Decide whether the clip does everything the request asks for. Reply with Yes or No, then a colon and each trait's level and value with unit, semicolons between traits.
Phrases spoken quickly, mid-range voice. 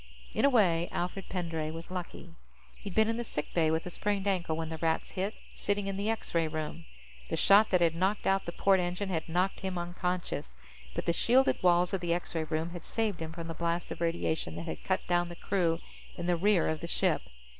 Yes: fast, 235 wpm; medium, 175 Hz